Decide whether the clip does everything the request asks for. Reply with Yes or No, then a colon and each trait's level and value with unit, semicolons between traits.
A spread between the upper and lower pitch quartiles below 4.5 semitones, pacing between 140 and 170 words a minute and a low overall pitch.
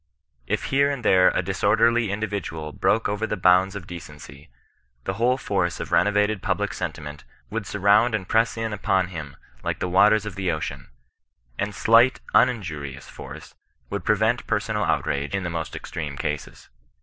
Yes: average, 4.0 semitones; average, 160 wpm; low, 100 Hz